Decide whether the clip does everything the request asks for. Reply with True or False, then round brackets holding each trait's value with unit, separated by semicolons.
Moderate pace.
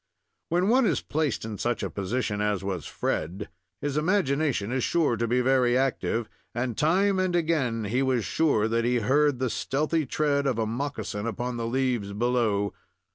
True (180 wpm)